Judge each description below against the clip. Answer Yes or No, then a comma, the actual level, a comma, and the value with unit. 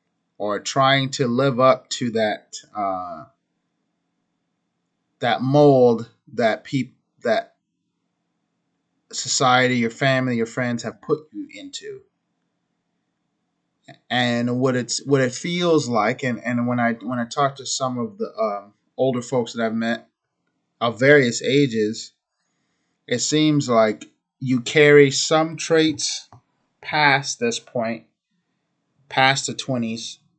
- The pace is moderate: No, slow, 120 wpm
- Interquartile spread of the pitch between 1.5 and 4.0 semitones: Yes, average, 3.7 semitones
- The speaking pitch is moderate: No, low, 130 Hz